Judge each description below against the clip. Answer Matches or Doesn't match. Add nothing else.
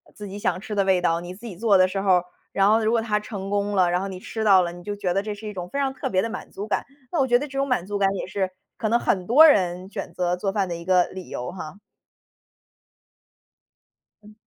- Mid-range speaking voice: Doesn't match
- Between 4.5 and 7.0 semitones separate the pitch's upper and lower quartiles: Doesn't match